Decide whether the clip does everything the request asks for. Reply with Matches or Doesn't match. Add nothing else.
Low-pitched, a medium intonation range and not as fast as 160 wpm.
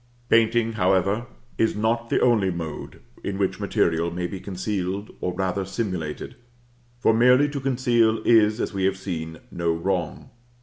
Matches